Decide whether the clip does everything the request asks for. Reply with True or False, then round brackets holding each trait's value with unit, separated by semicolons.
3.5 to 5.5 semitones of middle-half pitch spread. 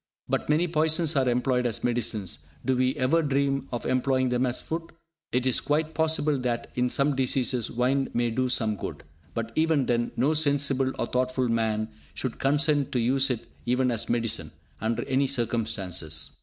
False (2.8 semitones)